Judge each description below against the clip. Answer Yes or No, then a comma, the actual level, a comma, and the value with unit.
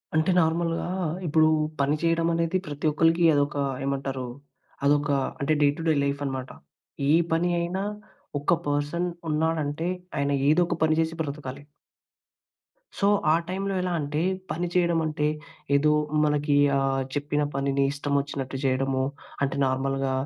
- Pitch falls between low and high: Yes, medium, 150 Hz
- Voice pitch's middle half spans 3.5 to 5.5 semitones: No, average, 2.8 semitones